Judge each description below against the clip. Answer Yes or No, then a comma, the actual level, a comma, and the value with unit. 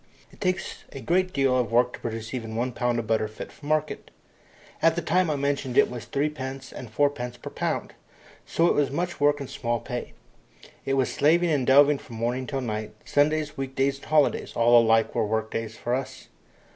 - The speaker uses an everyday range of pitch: Yes, average, 3.7 semitones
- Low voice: Yes, low, 130 Hz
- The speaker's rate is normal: No, fast, 210 wpm